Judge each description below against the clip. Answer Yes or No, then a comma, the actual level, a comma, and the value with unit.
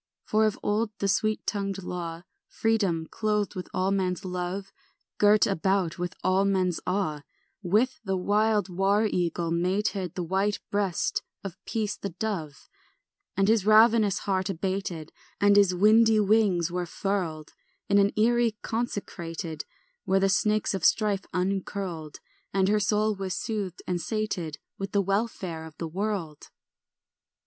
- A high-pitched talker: Yes, high, 195 Hz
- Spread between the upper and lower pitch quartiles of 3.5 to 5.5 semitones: No, average, 2.8 semitones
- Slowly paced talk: No, average, 145 wpm